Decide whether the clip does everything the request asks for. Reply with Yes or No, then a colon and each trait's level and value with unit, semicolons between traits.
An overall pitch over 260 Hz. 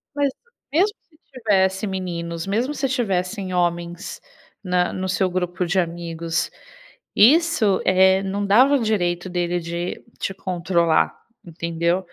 No: medium, 185 Hz